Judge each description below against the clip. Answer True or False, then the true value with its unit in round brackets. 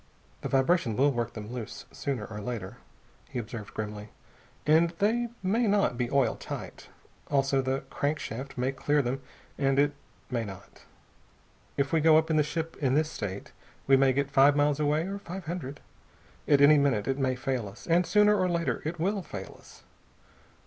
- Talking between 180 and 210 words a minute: True (185 wpm)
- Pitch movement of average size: True (4.4 semitones)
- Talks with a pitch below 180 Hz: True (140 Hz)